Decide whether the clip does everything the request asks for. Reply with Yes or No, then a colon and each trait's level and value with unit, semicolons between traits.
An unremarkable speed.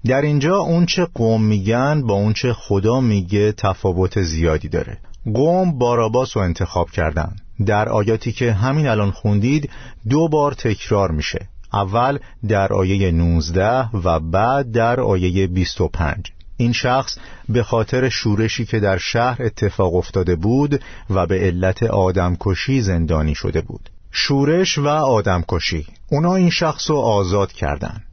Yes: average, 145 wpm